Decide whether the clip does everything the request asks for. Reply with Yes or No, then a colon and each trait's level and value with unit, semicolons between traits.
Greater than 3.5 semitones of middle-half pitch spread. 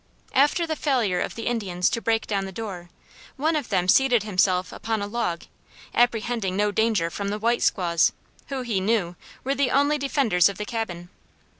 Yes: average, 4.5 semitones